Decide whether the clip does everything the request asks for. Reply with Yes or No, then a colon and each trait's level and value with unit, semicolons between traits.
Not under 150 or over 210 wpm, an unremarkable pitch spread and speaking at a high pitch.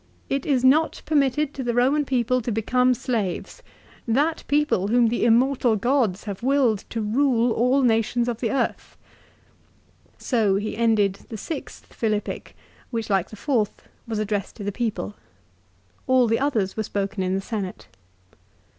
Yes: average, 165 wpm; average, 3.6 semitones; high, 235 Hz